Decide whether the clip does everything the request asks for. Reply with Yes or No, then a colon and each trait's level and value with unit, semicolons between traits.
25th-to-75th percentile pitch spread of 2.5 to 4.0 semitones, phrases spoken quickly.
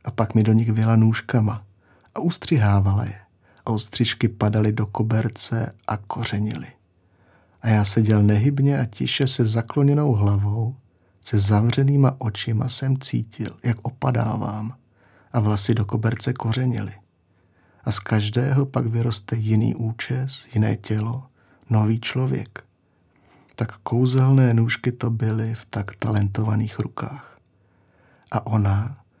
No: average, 2.8 semitones; average, 125 wpm